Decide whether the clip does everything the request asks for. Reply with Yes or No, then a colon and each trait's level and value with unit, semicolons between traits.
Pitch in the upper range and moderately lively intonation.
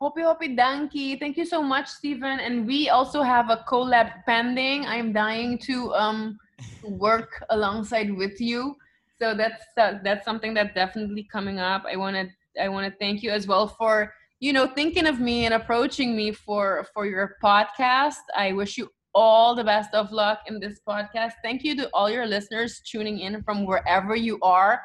Yes: high, 225 Hz; average, 3.5 semitones